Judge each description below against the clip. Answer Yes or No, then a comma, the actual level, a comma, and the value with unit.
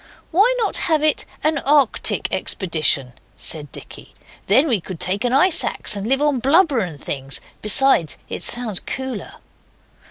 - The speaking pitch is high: Yes, high, 245 Hz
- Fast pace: No, average, 155 wpm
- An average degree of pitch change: No, wide, 8.2 semitones